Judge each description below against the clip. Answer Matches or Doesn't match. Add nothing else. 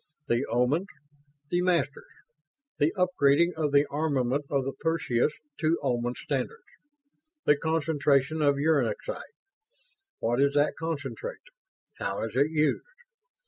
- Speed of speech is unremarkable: Doesn't match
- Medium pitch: Matches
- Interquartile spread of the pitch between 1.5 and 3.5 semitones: Matches